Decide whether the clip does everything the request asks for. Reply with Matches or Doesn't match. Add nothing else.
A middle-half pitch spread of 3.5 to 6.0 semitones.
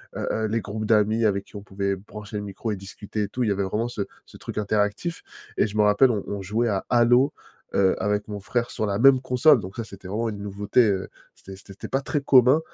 Doesn't match